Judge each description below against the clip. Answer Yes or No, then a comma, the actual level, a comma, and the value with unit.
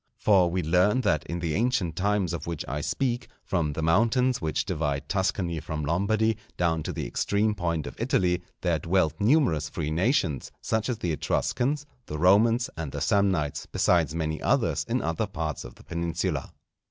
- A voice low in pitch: Yes, very low, 85 Hz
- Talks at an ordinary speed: Yes, average, 175 wpm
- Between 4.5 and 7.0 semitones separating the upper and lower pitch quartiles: Yes, average, 4.8 semitones